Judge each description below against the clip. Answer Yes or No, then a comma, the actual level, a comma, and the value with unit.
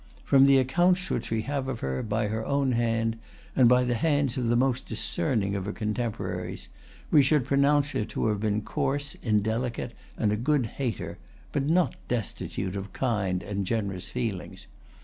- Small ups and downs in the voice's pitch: No, average, 4.3 semitones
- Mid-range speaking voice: No, low, 120 Hz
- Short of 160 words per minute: No, average, 175 wpm